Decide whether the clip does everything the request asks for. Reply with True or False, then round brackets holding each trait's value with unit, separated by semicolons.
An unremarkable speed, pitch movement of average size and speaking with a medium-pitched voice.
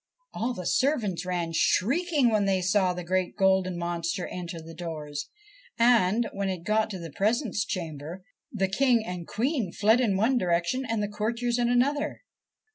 False (170 wpm; 5.0 semitones; 195 Hz)